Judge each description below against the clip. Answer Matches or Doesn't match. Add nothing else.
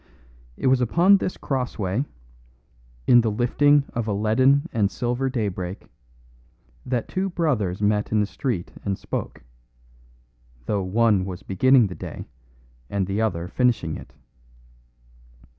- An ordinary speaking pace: Doesn't match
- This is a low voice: Matches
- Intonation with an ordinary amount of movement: Matches